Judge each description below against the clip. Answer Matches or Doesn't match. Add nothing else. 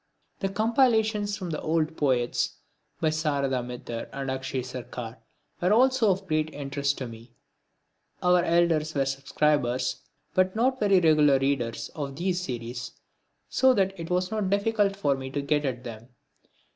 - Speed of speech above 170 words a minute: Doesn't match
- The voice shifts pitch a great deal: Matches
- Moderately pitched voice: Matches